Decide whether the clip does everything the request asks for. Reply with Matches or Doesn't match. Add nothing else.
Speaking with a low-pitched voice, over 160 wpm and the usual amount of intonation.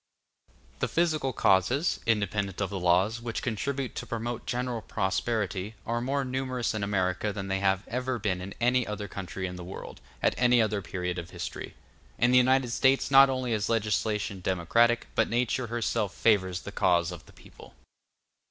Matches